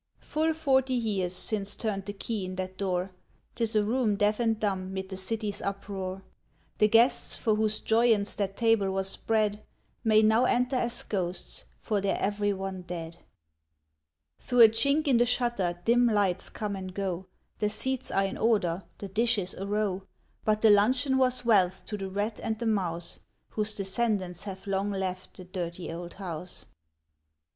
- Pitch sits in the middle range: No, high, 205 Hz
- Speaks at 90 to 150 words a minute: No, average, 175 wpm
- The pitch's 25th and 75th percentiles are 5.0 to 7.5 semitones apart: No, average, 3.0 semitones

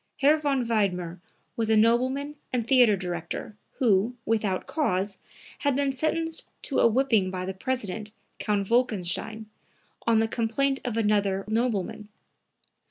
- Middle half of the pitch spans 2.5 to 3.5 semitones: No, average, 4.6 semitones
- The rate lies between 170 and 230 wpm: No, slow, 135 wpm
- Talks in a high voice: Yes, high, 225 Hz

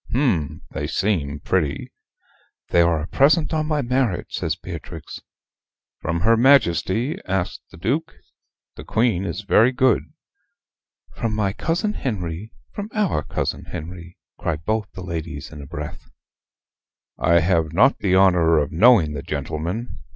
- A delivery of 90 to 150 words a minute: Yes, average, 145 wpm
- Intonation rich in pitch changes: Yes, wide, 6.5 semitones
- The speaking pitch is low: Yes, very low, 95 Hz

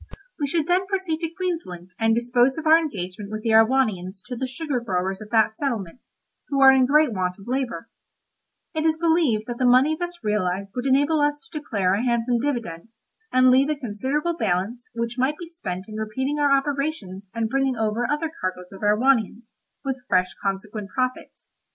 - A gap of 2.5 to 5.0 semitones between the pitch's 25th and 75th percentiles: No, wide, 5.6 semitones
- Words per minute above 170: Yes, average, 190 wpm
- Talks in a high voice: Yes, high, 245 Hz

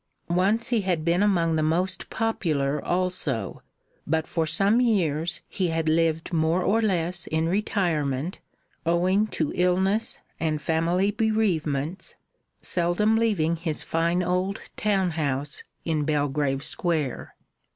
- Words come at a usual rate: No, slow, 125 wpm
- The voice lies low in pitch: No, medium, 170 Hz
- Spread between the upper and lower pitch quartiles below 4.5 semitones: Yes, average, 3.4 semitones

